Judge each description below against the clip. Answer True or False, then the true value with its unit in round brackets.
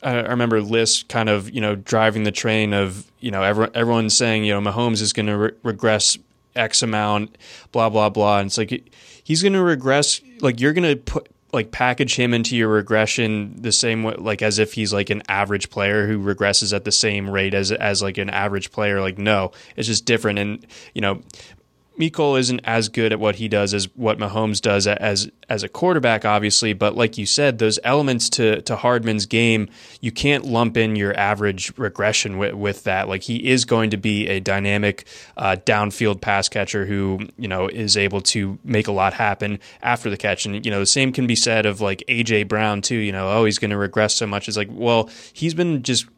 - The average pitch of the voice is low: True (110 Hz)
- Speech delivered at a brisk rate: True (215 wpm)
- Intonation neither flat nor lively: False (2.3 semitones)